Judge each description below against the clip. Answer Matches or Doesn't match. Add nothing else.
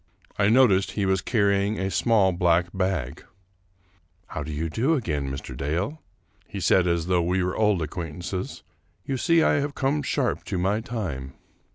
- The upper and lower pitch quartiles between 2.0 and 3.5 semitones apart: Doesn't match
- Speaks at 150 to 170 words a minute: Doesn't match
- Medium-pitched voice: Doesn't match